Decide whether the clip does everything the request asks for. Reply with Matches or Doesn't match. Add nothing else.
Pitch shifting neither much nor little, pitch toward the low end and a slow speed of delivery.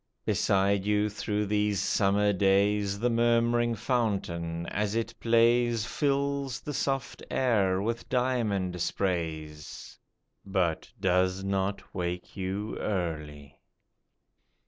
Matches